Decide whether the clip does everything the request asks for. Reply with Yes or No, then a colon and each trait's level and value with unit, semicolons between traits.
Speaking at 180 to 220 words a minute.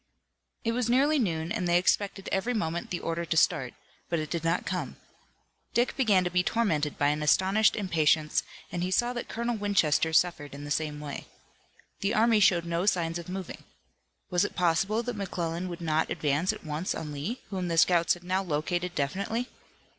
Yes: average, 190 wpm